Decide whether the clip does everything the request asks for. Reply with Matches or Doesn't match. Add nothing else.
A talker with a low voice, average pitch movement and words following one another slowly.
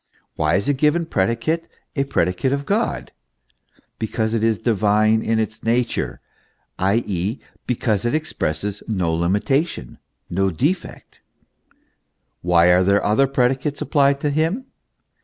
Doesn't match